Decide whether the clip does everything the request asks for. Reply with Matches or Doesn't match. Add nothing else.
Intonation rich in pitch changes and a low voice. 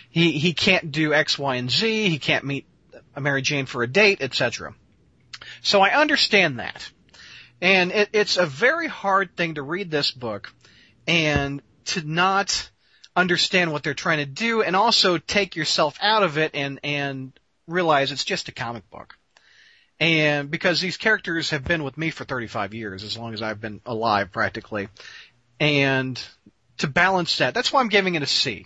Doesn't match